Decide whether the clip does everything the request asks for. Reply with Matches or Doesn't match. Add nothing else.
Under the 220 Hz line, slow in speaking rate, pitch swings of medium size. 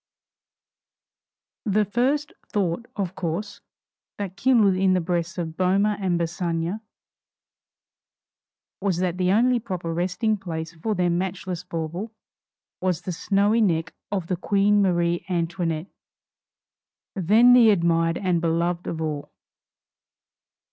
Matches